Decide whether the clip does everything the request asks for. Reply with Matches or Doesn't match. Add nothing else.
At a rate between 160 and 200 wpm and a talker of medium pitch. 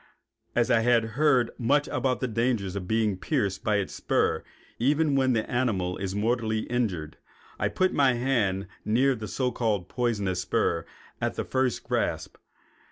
Doesn't match